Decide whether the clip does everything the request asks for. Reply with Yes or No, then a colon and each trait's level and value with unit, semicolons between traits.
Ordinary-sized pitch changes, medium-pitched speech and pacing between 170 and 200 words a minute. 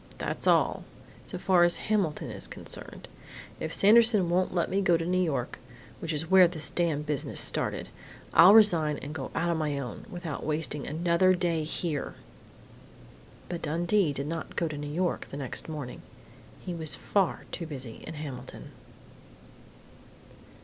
No: average, 3.2 semitones; medium, 165 Hz; average, 155 wpm